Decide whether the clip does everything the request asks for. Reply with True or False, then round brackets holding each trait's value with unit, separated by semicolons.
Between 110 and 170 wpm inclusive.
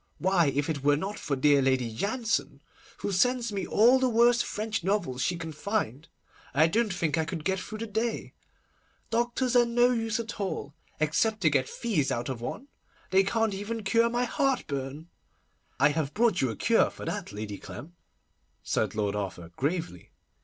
False (180 wpm)